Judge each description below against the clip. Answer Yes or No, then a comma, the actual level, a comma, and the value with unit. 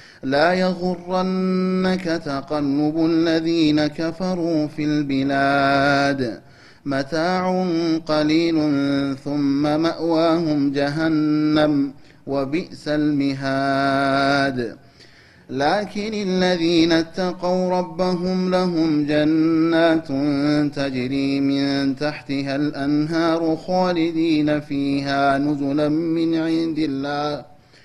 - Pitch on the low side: No, medium, 150 Hz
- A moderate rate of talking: No, slow, 65 wpm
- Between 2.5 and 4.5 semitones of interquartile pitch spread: Yes, average, 2.9 semitones